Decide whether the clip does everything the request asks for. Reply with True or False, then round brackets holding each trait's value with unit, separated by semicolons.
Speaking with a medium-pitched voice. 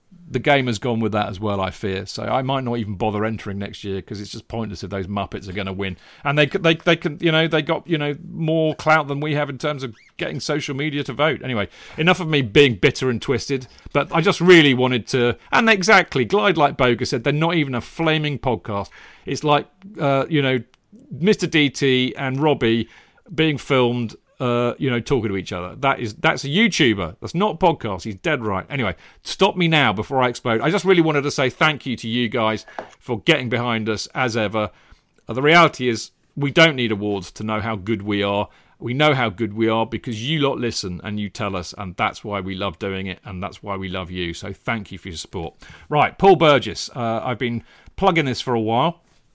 False (125 Hz)